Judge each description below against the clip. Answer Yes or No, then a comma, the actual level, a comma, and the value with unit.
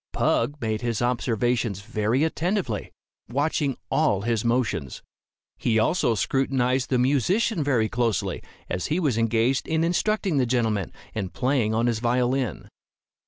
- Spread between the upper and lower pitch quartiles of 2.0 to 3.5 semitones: No, average, 3.9 semitones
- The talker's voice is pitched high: No, low, 125 Hz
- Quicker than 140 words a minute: No, slow, 135 wpm